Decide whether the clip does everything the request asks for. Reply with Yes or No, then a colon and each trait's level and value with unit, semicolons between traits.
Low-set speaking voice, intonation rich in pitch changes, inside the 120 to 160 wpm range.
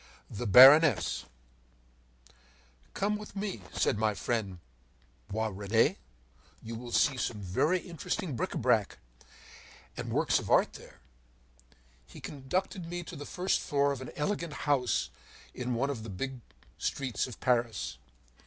Yes: low, 130 Hz; wide, 5.8 semitones; slow, 135 wpm